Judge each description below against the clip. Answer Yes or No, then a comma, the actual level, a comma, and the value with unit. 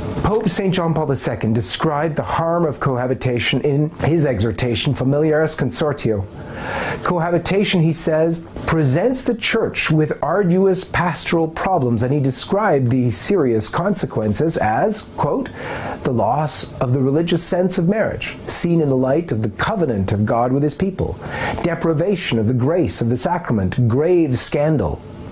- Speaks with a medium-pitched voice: Yes, medium, 150 Hz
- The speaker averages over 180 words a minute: No, average, 145 wpm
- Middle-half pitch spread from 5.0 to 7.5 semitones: Yes, wide, 5.4 semitones